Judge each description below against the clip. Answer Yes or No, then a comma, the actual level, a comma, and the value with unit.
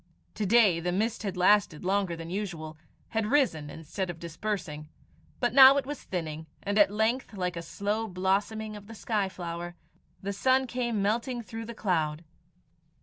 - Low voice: No, high, 200 Hz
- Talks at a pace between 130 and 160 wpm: No, average, 170 wpm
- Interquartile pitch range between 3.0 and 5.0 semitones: Yes, average, 4.4 semitones